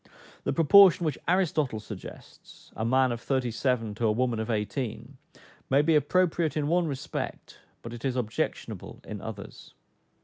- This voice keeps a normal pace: Yes, average, 160 wpm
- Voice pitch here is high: No, low, 130 Hz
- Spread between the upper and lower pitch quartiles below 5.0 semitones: No, wide, 5.5 semitones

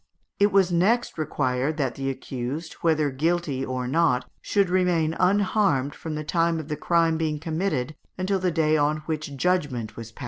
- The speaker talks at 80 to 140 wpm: No, average, 175 wpm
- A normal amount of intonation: Yes, average, 4.2 semitones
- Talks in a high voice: No, medium, 155 Hz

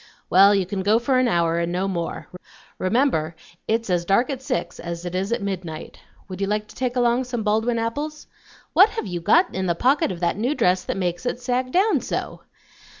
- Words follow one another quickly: Yes, fast, 215 wpm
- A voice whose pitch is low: No, high, 210 Hz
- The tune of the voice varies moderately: No, wide, 5.8 semitones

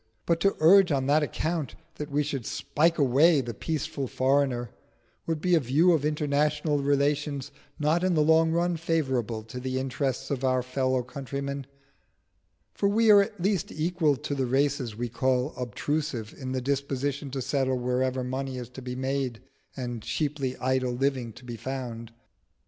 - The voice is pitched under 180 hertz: Yes, medium, 140 Hz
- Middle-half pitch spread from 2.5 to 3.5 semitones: Yes, average, 3.0 semitones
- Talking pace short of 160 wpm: No, average, 170 wpm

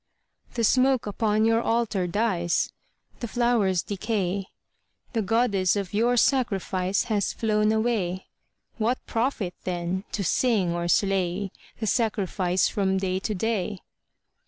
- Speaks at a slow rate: Yes, slow, 130 wpm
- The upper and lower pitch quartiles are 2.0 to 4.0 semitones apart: Yes, average, 3.4 semitones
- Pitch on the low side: No, high, 205 Hz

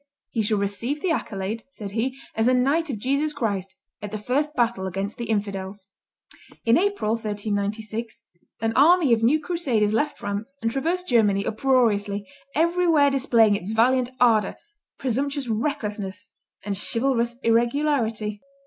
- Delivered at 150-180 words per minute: No, average, 140 wpm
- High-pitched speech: Yes, high, 230 Hz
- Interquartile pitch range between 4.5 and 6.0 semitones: Yes, average, 4.8 semitones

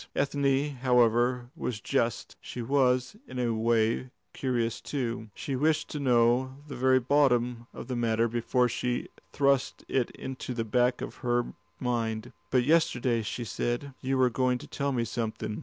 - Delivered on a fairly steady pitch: Yes, narrow, 2.0 semitones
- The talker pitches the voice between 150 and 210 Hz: No, low, 125 Hz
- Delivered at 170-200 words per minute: No, average, 160 wpm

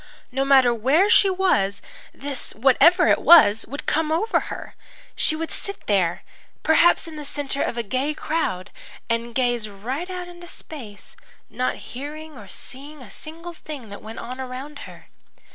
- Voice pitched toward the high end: Yes, very high, 275 Hz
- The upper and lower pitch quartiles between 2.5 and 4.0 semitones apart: No, average, 5.2 semitones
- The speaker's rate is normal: Yes, average, 165 wpm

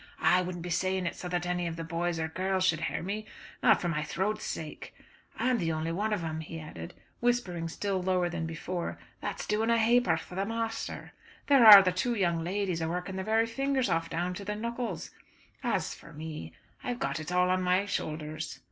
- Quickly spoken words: Yes, fast, 220 wpm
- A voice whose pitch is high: No, medium, 180 Hz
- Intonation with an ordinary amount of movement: Yes, average, 4.1 semitones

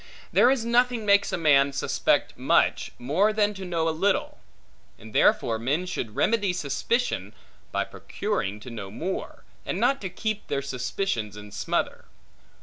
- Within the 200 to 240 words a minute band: No, average, 150 wpm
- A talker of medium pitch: Yes, medium, 175 Hz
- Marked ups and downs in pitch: Yes, wide, 8.7 semitones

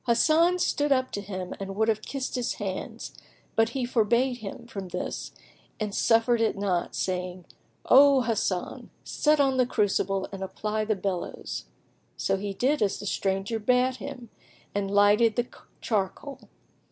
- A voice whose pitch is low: No, high, 220 Hz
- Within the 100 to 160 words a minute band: Yes, average, 155 wpm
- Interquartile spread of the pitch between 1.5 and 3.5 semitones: No, average, 4.3 semitones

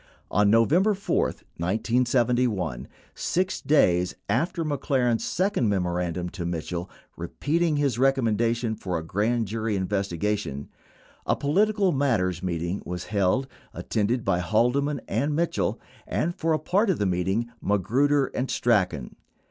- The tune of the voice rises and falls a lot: Yes, wide, 7.5 semitones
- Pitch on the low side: Yes, low, 115 Hz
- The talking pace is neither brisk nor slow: No, slow, 130 wpm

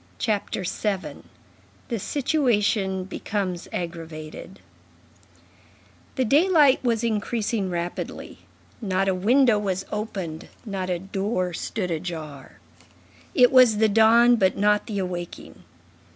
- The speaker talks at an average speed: No, slow, 105 wpm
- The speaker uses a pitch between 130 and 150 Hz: No, high, 200 Hz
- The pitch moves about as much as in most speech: Yes, average, 3.9 semitones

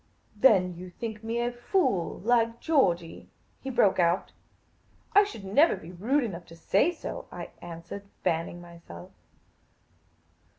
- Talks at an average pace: Yes, average, 155 wpm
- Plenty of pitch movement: Yes, wide, 5.7 semitones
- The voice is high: Yes, high, 200 Hz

